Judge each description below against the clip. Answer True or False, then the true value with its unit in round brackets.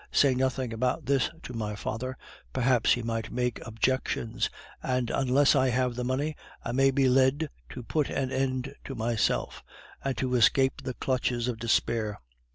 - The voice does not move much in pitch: True (2.1 semitones)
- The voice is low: True (125 Hz)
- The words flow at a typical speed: True (165 wpm)